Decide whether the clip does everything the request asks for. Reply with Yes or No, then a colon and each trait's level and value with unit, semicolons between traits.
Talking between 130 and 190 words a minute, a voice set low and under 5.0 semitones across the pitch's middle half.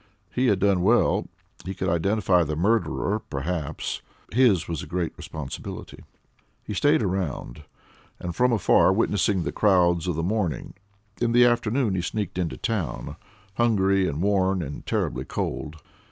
Yes: average, 150 wpm; very low, 95 Hz; average, 4.3 semitones